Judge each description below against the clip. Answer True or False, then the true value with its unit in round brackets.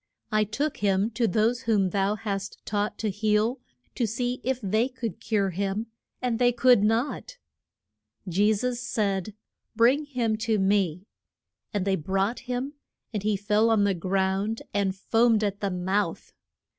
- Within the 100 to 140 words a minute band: False (155 wpm)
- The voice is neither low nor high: False (215 Hz)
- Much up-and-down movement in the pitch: False (3.0 semitones)